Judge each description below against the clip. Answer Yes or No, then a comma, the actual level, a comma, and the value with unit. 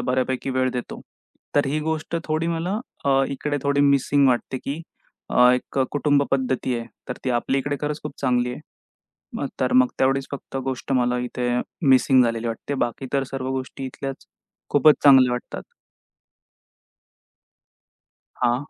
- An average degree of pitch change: No, narrow, 2.3 semitones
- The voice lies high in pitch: No, low, 135 Hz